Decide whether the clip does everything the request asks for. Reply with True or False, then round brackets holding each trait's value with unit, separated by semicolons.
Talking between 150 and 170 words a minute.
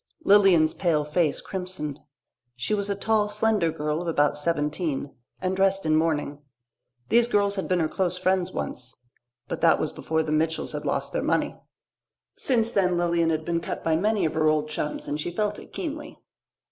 False (185 wpm)